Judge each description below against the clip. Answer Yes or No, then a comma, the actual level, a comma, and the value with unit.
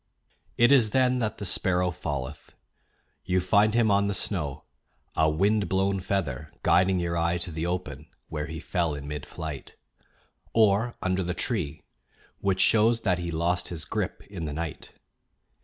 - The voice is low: Yes, very low, 90 Hz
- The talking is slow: No, average, 165 wpm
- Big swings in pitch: No, average, 3.9 semitones